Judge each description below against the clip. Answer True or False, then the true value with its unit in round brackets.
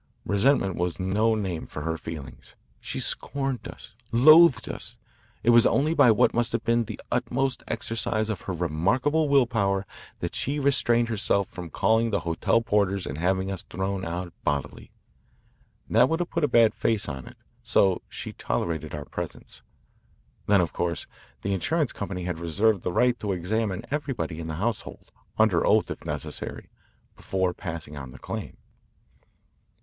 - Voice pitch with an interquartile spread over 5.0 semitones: True (5.4 semitones)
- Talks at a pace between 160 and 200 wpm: True (165 wpm)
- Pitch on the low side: True (100 Hz)